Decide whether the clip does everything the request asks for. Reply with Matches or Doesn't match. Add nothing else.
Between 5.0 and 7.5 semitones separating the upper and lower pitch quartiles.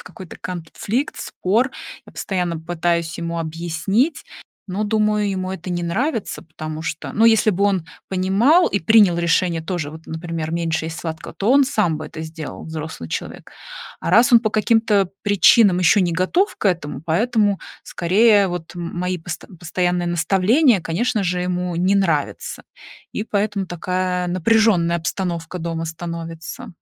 Doesn't match